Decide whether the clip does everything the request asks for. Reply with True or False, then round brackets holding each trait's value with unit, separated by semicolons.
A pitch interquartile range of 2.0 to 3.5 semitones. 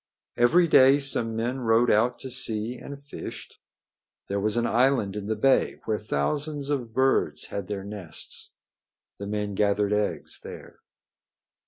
False (4.2 semitones)